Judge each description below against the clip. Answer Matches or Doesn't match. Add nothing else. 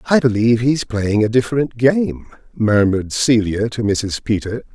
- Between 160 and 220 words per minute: Doesn't match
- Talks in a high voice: Doesn't match